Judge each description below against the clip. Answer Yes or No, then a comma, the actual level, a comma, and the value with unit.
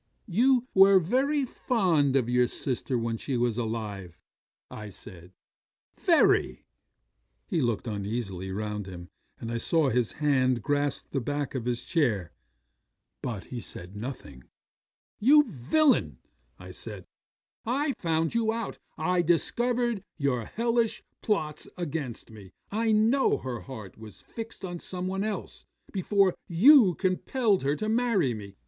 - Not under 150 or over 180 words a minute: No, average, 140 wpm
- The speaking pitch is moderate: Yes, medium, 145 Hz